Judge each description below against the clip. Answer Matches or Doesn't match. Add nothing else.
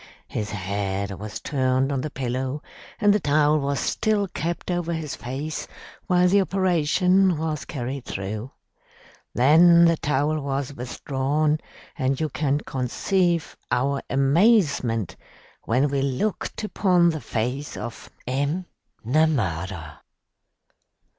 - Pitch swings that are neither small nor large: Matches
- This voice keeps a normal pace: Doesn't match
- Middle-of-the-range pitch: Matches